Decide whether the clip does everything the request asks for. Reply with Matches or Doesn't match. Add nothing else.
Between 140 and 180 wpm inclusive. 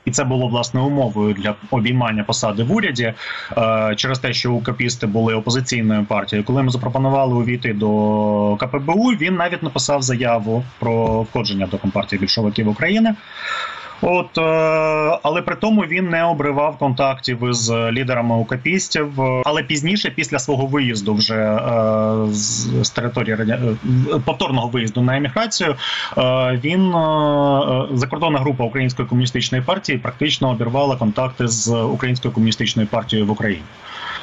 Doesn't match